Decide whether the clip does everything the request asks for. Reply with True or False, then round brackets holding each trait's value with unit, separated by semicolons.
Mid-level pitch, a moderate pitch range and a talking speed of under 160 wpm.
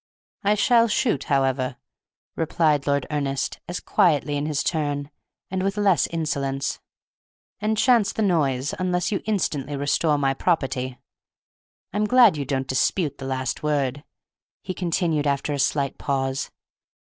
True (150 Hz; 4.9 semitones; 145 wpm)